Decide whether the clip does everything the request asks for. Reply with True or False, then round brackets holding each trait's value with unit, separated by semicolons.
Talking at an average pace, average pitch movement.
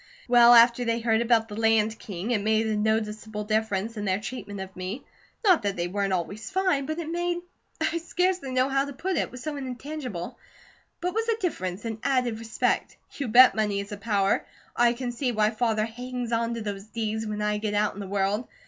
False (225 wpm; 3.5 semitones)